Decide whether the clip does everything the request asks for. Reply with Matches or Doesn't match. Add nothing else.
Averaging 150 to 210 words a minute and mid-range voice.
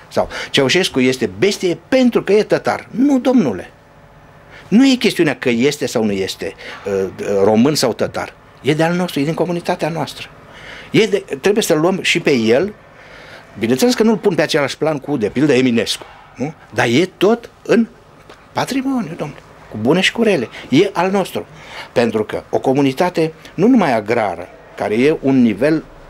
Matches